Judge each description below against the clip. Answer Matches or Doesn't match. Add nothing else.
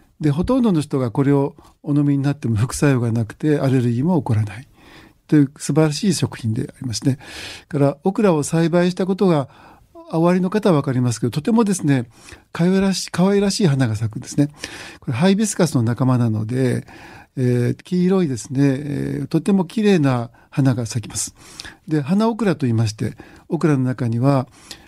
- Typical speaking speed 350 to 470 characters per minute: Matches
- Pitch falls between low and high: Matches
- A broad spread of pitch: Matches